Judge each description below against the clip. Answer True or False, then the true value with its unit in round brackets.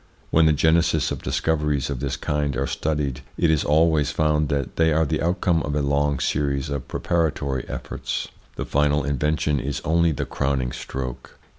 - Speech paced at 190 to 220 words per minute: False (180 wpm)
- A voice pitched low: True (75 Hz)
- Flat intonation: True (2.2 semitones)